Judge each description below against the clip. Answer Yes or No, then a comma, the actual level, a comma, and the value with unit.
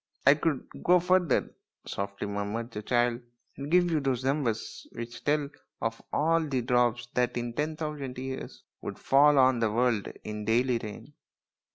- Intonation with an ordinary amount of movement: Yes, average, 4.1 semitones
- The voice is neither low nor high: No, low, 125 Hz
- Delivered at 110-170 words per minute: No, average, 180 wpm